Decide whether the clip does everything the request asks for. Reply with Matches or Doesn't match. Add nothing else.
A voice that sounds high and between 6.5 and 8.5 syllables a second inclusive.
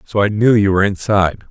Doesn't match